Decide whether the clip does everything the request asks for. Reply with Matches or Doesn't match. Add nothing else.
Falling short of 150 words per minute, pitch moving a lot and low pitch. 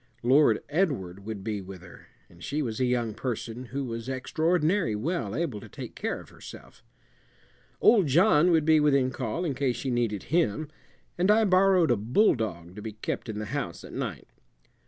Doesn't match